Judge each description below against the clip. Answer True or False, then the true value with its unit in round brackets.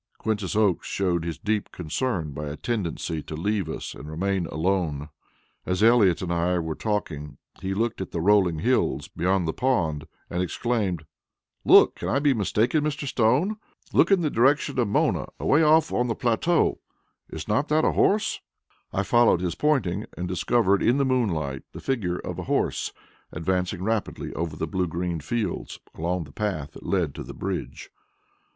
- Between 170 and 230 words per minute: True (175 wpm)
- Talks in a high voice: False (95 Hz)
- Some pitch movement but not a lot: False (5.9 semitones)